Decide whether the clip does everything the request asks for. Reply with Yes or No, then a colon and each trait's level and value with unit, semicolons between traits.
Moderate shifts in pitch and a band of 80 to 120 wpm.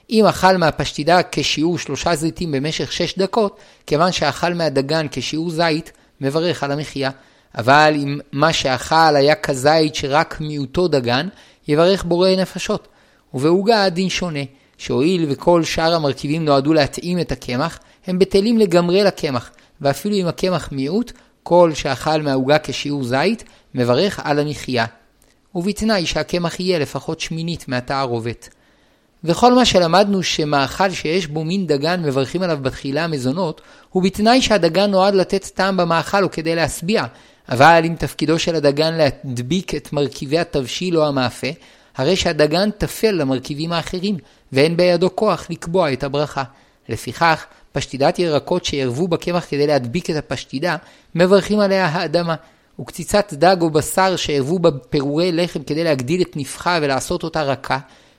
No: average, 4.1 semitones; average, 135 wpm